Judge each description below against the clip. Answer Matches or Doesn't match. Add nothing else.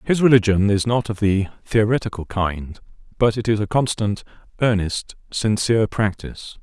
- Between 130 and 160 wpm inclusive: Matches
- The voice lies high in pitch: Doesn't match